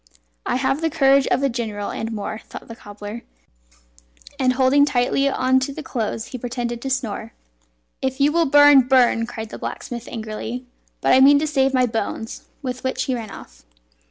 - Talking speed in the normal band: Yes, average, 185 wpm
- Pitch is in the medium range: No, very high, 255 Hz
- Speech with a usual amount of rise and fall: Yes, average, 3.0 semitones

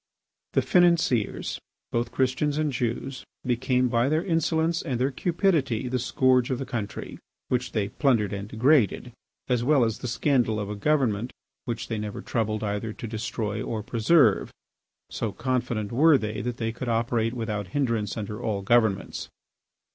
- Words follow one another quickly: No, average, 160 wpm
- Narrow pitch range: No, average, 3.4 semitones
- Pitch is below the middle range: Yes, low, 120 Hz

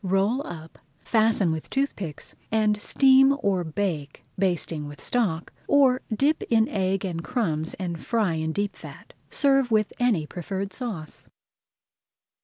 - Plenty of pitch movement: Yes, wide, 6.2 semitones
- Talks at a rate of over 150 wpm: No, slow, 135 wpm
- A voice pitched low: No, high, 200 Hz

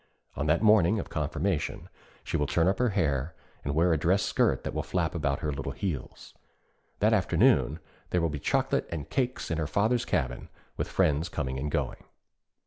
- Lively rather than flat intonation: No, average, 4.5 semitones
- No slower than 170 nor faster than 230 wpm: Yes, average, 195 wpm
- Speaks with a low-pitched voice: Yes, very low, 80 Hz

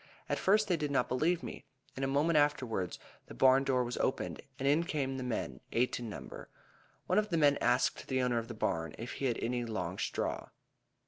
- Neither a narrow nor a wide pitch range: Yes, average, 3.4 semitones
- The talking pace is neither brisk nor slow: No, fast, 215 wpm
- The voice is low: Yes, low, 130 Hz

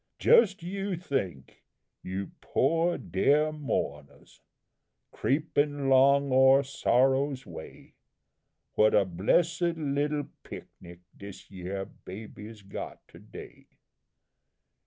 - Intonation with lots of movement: Yes, wide, 7.2 semitones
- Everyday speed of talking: No, slow, 95 wpm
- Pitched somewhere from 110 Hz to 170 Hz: Yes, low, 135 Hz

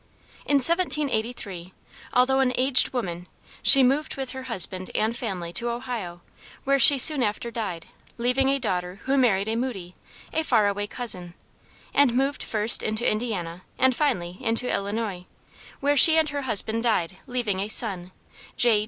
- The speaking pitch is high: Yes, high, 235 Hz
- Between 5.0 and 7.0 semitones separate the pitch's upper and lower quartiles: Yes, average, 5.3 semitones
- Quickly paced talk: No, average, 160 wpm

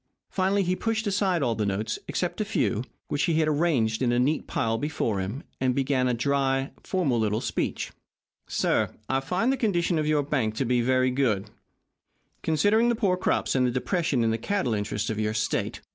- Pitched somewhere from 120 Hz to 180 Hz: Yes, low, 135 Hz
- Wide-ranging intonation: Yes, wide, 7.3 semitones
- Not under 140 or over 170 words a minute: No, average, 195 wpm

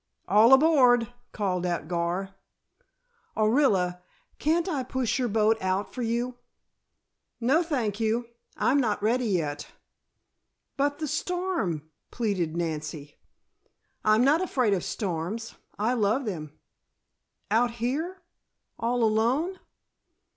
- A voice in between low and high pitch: No, high, 230 Hz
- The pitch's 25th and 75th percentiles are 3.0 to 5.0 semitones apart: No, wide, 5.6 semitones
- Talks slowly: Yes, slow, 110 wpm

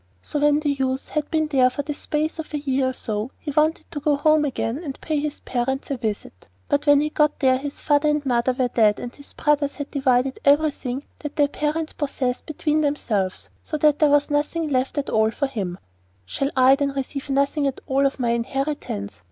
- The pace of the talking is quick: Yes, fast, 215 wpm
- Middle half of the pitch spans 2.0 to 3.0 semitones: Yes, narrow, 2.5 semitones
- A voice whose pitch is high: Yes, very high, 280 Hz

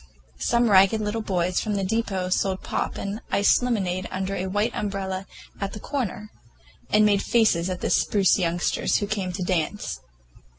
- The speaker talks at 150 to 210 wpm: Yes, average, 170 wpm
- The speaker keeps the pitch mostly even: Yes, narrow, 2.3 semitones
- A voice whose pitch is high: Yes, high, 195 Hz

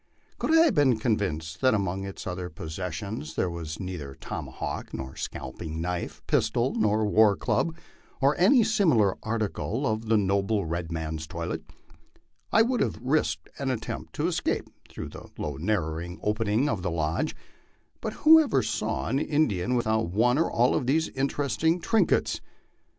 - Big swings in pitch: Yes, wide, 7.5 semitones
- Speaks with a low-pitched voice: Yes, low, 110 Hz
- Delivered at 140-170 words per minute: Yes, average, 165 wpm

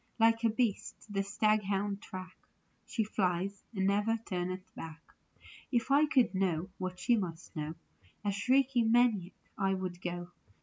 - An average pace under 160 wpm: Yes, average, 145 wpm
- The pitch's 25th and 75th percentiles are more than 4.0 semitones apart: No, average, 3.6 semitones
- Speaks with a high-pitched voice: Yes, high, 195 Hz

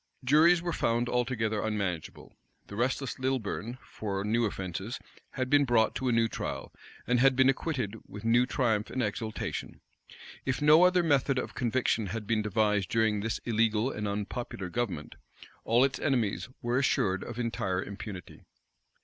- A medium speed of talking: Yes, average, 160 wpm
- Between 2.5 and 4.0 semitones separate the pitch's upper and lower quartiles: Yes, average, 3.6 semitones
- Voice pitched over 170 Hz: No, low, 115 Hz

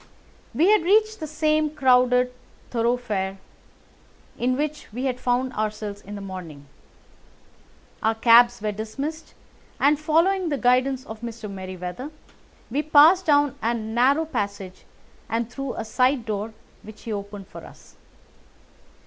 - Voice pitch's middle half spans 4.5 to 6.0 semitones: Yes, average, 5.3 semitones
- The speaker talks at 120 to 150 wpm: Yes, slow, 135 wpm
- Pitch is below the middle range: No, high, 245 Hz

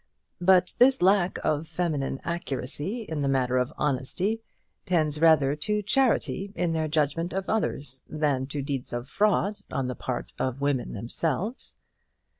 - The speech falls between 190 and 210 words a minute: No, average, 150 wpm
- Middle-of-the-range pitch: Yes, medium, 155 Hz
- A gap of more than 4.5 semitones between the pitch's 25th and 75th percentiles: Yes, wide, 5.5 semitones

